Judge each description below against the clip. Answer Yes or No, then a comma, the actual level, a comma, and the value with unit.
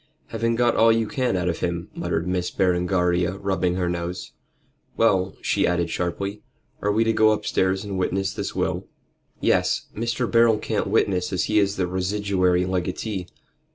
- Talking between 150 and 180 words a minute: Yes, average, 165 wpm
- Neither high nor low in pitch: No, very low, 95 Hz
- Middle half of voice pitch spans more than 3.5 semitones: No, average, 3.1 semitones